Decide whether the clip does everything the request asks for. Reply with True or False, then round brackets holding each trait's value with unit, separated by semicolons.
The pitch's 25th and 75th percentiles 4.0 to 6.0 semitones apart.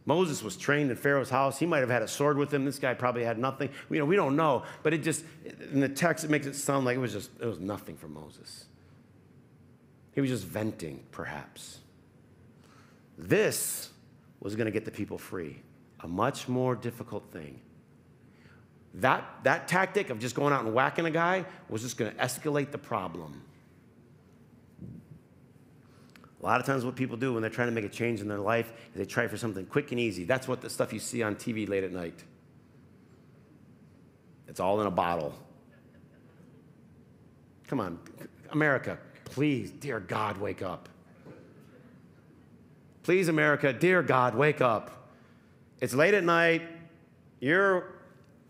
True (4.9 semitones)